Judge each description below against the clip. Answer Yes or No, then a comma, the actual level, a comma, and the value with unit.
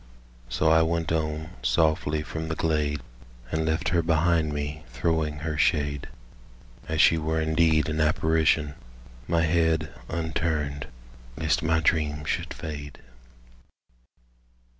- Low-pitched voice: Yes, very low, 80 Hz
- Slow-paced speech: Yes, slow, 120 wpm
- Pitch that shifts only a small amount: Yes, narrow, 1.2 semitones